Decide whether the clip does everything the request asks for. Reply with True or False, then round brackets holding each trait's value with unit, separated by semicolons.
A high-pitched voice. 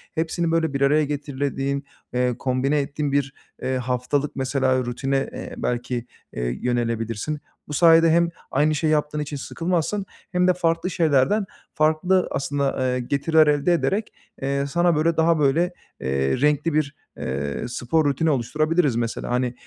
False (145 Hz)